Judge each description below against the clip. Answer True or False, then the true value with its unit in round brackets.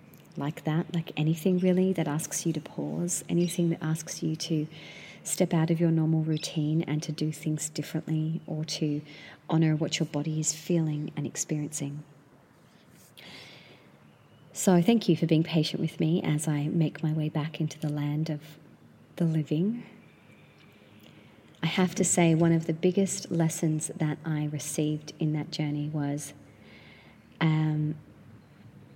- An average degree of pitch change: False (1.8 semitones)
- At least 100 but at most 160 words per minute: True (150 wpm)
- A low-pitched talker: False (155 Hz)